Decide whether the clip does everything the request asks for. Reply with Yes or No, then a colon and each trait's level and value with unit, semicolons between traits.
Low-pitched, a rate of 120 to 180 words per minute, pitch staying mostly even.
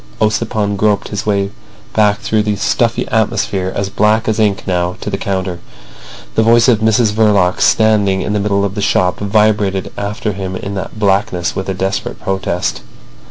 Yes: low, 100 Hz; average, 175 wpm; narrow, 1.9 semitones